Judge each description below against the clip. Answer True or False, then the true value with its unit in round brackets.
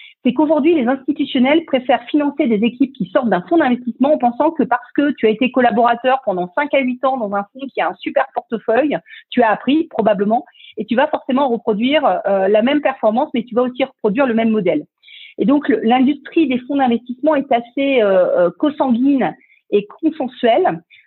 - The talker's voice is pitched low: False (260 Hz)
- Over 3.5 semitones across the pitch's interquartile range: True (3.9 semitones)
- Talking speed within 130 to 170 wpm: False (195 wpm)